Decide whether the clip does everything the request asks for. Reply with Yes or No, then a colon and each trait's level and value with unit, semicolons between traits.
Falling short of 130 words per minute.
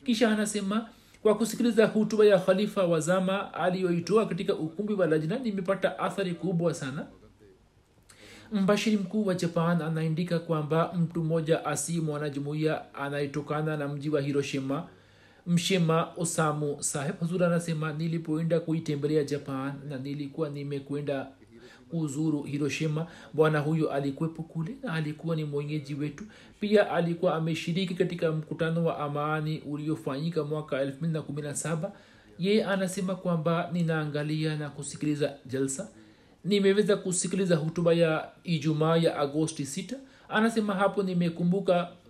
Yes: average, 115 wpm